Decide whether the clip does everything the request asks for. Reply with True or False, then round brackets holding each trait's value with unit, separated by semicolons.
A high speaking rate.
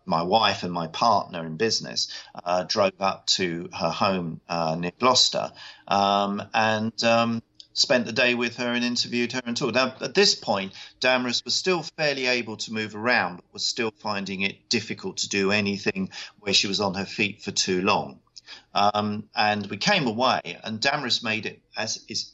False (190 wpm)